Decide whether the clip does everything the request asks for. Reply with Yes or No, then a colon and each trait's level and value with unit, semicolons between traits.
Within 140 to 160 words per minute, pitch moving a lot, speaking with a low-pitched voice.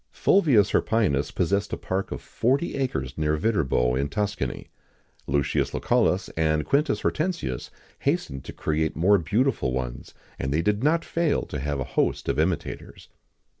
Yes: average, 150 wpm; wide, 8.7 semitones; very low, 85 Hz